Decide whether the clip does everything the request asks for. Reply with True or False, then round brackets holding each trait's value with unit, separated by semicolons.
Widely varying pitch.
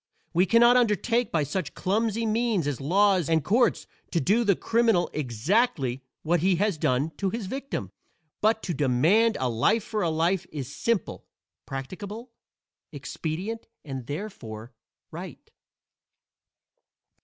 True (7.2 semitones)